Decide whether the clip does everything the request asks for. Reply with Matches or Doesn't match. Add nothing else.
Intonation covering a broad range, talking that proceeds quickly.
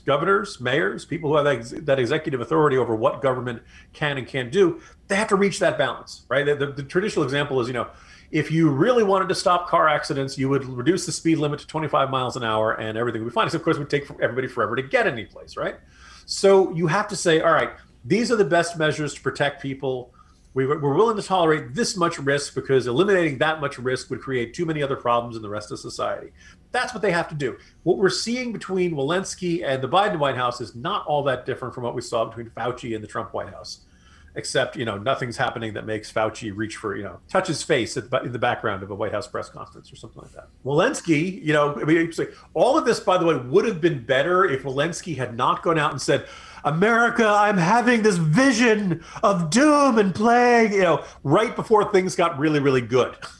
Matches